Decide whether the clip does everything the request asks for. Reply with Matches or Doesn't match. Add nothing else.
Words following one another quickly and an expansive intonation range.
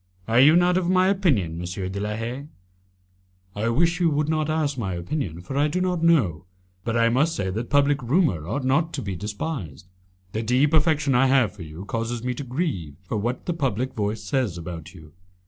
Matches